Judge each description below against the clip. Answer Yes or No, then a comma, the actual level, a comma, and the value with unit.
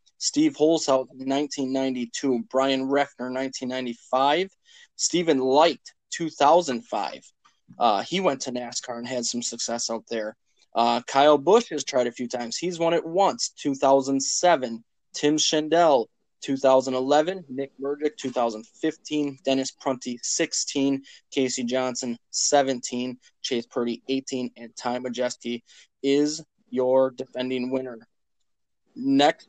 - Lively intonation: No, average, 3.3 semitones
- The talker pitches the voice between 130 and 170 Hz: Yes, low, 135 Hz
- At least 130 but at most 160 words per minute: Yes, average, 140 wpm